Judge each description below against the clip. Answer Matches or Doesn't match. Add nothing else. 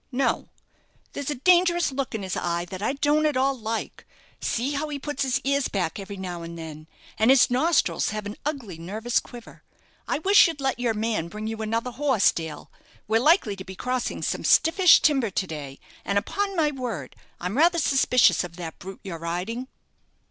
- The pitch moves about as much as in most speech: Doesn't match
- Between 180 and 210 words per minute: Matches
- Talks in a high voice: Matches